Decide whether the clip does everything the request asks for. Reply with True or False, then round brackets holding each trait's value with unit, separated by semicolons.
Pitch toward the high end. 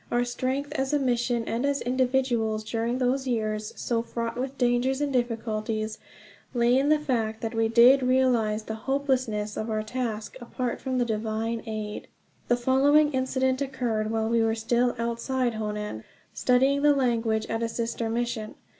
True (240 Hz)